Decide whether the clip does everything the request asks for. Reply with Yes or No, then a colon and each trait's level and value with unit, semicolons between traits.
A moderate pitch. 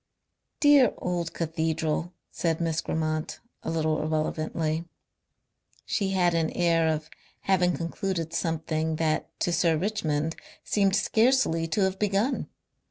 Yes: medium, 165 Hz